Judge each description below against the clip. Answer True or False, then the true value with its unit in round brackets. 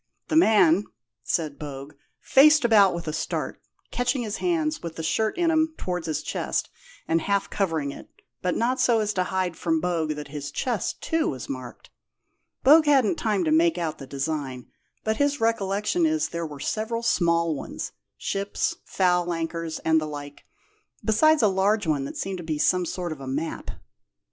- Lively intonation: True (6.2 semitones)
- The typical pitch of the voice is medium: True (180 Hz)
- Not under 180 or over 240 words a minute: True (185 wpm)